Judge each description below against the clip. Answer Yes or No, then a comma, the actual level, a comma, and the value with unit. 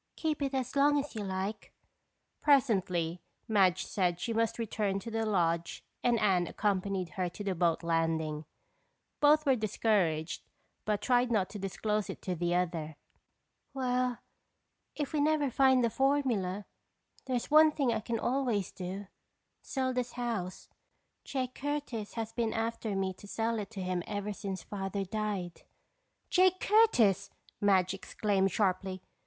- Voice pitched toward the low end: No, high, 210 Hz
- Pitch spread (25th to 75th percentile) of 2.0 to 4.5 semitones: No, average, 5.0 semitones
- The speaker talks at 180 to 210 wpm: No, average, 150 wpm